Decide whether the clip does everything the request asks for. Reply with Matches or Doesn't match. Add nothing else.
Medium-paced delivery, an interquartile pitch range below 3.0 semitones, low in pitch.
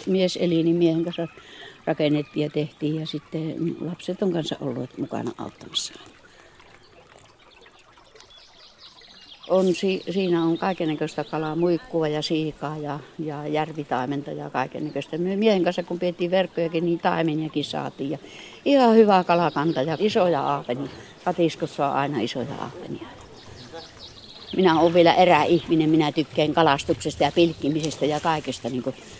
Doesn't match